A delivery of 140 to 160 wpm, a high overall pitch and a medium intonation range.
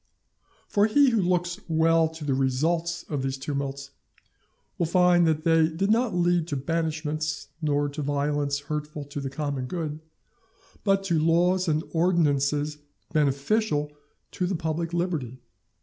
No: average, 145 wpm; medium, 160 Hz; average, 3.2 semitones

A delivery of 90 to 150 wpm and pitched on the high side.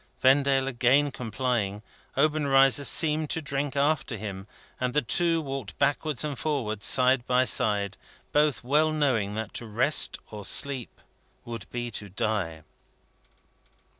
No: slow, 135 wpm; low, 130 Hz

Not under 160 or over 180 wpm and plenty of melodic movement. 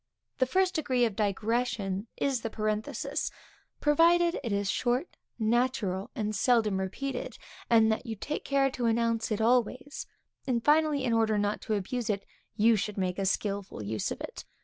No: average, 170 wpm; average, 3.9 semitones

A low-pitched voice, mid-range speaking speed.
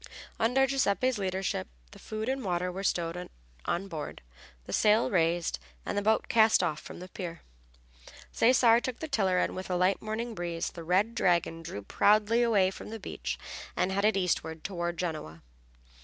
No: high, 190 Hz; average, 170 wpm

